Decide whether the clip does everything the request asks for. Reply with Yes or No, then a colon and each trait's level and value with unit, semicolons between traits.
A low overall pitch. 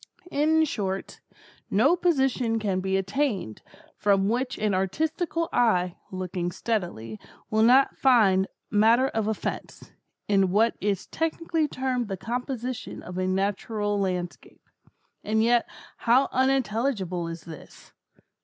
No: high, 215 Hz